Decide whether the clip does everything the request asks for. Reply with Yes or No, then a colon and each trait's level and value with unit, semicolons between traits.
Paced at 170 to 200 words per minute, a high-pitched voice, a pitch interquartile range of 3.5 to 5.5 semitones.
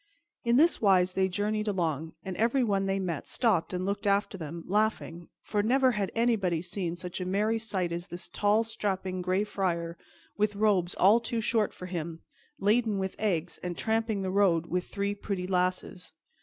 No: average, 180 wpm; high, 195 Hz; average, 2.9 semitones